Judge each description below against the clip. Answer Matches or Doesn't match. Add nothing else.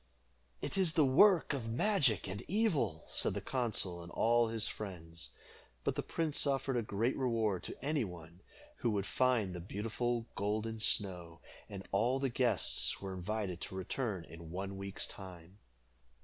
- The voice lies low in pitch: Matches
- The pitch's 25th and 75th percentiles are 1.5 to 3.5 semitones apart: Doesn't match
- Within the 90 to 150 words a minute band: Doesn't match